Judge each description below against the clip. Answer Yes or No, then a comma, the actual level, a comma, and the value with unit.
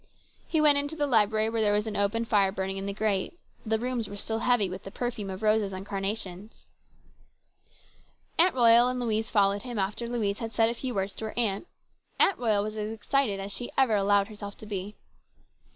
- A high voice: Yes, high, 215 Hz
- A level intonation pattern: No, average, 3.0 semitones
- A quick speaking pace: Yes, fast, 210 wpm